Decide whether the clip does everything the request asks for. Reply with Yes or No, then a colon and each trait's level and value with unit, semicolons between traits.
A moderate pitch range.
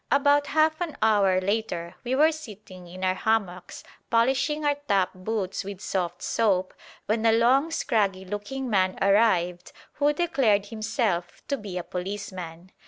No: wide, 5.8 semitones